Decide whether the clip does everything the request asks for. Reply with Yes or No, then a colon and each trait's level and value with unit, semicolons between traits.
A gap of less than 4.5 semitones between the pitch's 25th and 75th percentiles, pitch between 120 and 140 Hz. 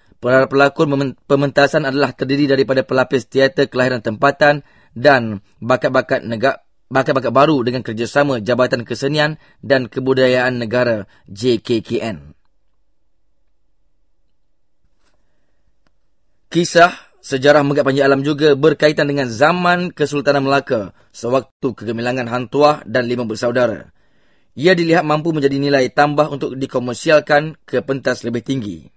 Yes: average, 2.8 semitones; low, 135 Hz